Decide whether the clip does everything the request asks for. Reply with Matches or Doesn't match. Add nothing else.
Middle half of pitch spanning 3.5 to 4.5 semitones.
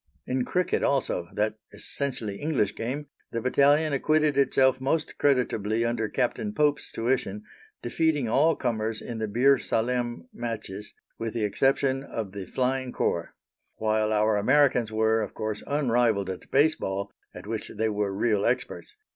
Matches